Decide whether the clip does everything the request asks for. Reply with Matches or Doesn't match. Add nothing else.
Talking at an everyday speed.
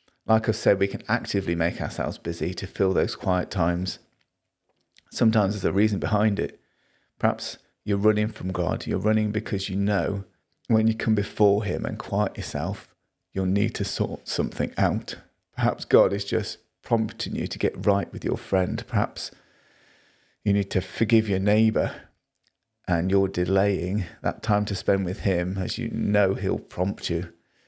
Matches